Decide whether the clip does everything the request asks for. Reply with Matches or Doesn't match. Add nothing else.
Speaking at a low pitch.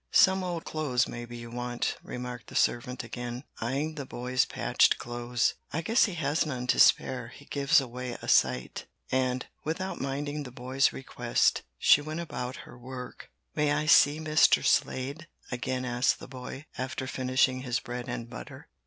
Matches